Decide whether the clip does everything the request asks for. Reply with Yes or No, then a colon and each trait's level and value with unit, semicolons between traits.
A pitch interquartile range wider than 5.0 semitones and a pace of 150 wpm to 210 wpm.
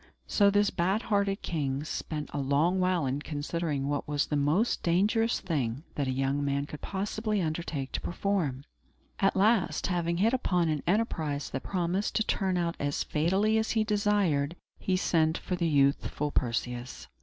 Yes: wide, 5.5 semitones; average, 170 wpm